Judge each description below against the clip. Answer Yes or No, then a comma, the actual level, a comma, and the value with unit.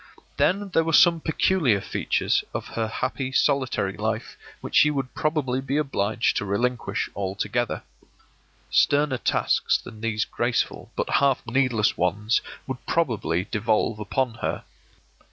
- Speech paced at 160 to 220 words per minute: No, slow, 135 wpm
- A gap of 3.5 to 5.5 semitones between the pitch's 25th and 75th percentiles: Yes, average, 4.7 semitones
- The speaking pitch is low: Yes, low, 120 Hz